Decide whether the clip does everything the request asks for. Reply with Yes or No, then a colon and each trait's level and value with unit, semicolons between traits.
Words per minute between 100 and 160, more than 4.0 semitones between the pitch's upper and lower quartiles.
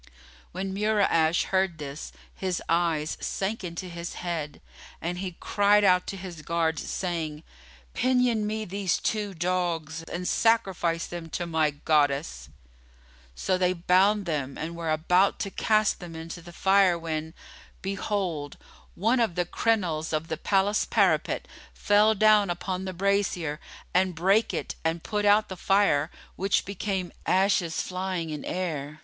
No: average, 145 wpm; average, 3.4 semitones